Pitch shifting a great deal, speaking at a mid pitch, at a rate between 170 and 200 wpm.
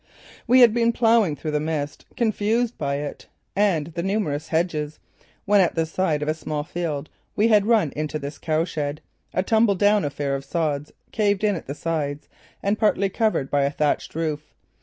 Yes: wide, 5.7 semitones; medium, 165 Hz; average, 180 wpm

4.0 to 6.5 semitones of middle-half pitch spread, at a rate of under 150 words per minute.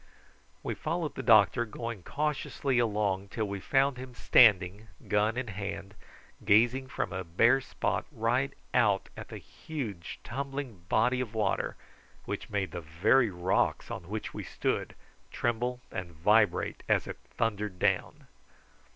Yes: average, 4.3 semitones; average, 140 wpm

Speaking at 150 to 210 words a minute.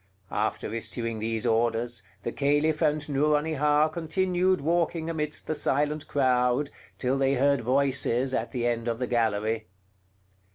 No: slow, 135 wpm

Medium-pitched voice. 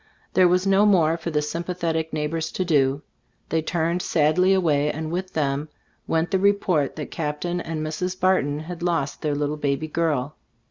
Yes: medium, 160 Hz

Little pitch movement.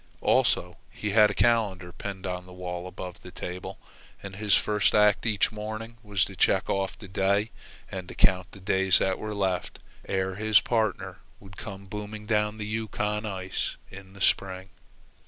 Yes: narrow, 2.0 semitones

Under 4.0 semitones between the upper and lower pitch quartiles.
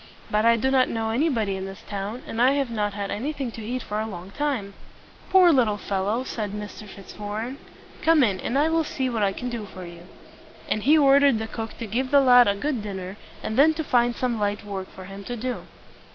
No: average, 4.3 semitones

